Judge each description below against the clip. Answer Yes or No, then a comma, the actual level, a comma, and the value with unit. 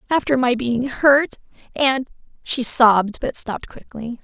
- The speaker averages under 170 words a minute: Yes, average, 140 wpm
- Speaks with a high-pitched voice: Yes, very high, 250 Hz